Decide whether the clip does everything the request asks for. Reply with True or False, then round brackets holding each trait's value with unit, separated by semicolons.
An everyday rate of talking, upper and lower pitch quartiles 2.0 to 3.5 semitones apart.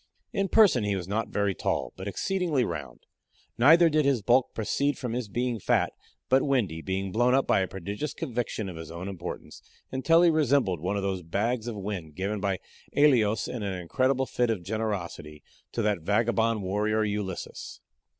False (180 wpm; 5.0 semitones)